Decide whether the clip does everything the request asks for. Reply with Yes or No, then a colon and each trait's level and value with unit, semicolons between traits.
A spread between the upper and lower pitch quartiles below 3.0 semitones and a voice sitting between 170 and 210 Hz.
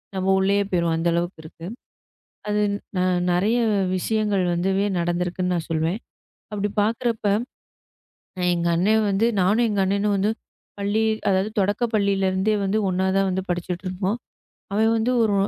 Yes: narrow, 2.6 semitones; high, 195 Hz